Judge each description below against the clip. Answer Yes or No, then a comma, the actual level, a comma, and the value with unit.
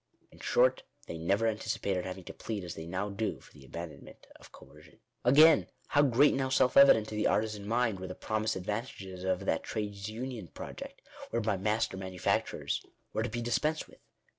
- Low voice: Yes, low, 105 Hz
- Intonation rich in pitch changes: No, average, 4.1 semitones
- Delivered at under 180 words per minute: No, average, 190 wpm